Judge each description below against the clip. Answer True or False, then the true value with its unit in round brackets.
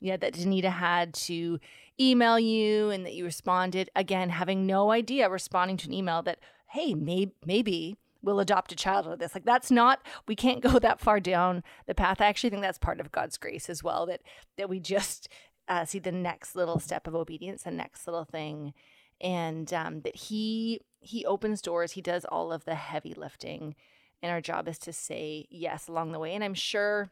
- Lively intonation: False (3.5 semitones)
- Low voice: False (185 Hz)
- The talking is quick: True (210 wpm)